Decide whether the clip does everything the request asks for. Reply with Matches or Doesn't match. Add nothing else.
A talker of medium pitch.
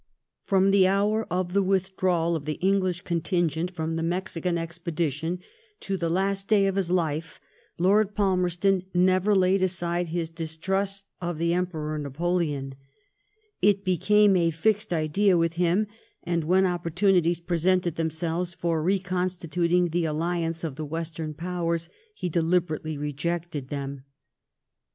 Matches